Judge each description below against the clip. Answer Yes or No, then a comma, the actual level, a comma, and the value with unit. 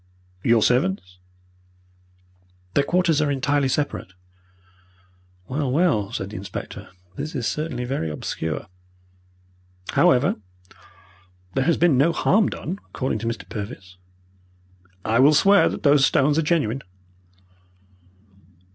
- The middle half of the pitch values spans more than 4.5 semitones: Yes, wide, 5.5 semitones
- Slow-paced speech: Yes, slow, 115 wpm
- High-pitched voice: No, low, 135 Hz